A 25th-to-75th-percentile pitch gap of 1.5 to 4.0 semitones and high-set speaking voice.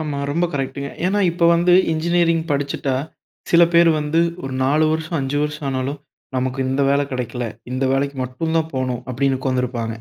No: average, 3.7 semitones; medium, 140 Hz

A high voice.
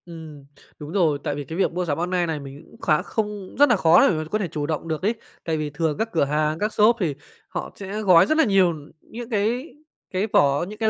No: medium, 175 Hz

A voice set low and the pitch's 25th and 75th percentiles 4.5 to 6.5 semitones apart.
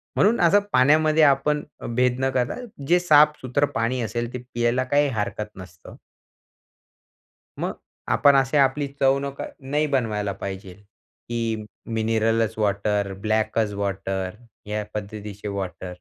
Yes: low, 115 Hz; average, 5.0 semitones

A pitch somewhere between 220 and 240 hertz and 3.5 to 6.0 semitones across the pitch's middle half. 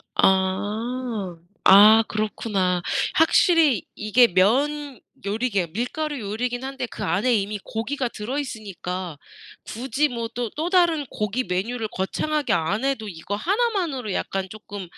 Yes: high, 225 Hz; average, 5.3 semitones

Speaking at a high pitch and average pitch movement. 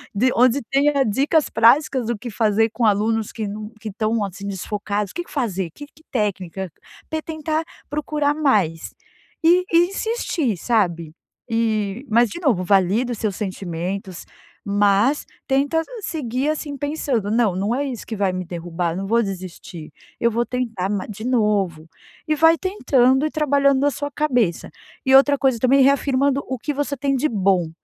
No: high, 235 Hz; wide, 6.0 semitones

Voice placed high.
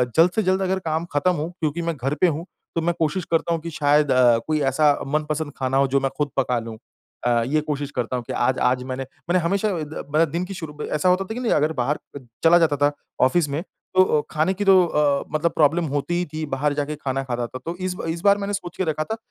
No: medium, 155 Hz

